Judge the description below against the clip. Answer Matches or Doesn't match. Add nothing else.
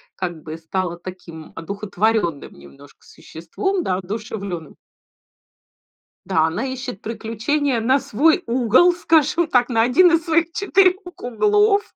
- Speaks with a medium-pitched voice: Doesn't match